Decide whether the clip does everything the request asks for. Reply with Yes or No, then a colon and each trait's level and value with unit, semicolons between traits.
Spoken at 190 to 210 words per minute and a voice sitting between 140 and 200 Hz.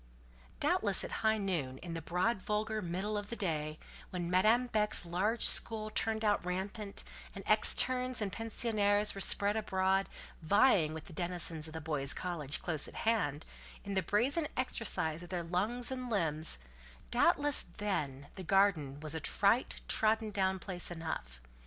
No: average, 160 wpm; high, 190 Hz